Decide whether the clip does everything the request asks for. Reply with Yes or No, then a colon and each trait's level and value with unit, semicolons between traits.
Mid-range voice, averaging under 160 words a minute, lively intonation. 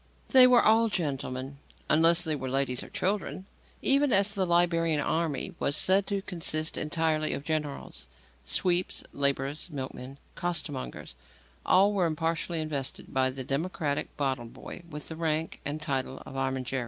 No: medium, 155 Hz; average, 150 wpm; average, 4.2 semitones